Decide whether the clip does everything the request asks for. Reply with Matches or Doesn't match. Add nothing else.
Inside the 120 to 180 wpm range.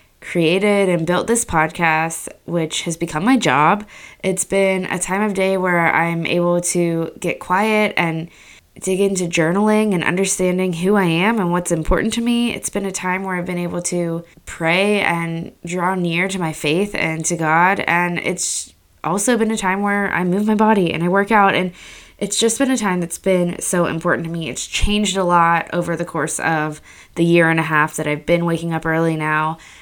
Doesn't match